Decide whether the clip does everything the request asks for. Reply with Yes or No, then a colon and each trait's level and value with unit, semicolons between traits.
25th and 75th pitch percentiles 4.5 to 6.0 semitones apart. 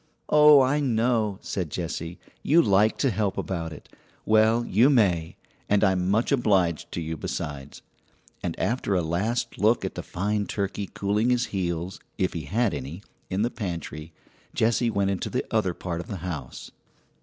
Yes: average, 4.9 semitones